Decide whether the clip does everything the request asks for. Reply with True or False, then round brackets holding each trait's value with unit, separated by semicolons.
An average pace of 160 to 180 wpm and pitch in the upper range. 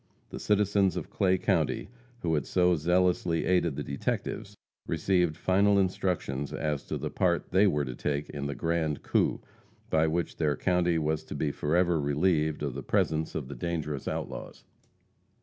False (165 wpm; 80 Hz)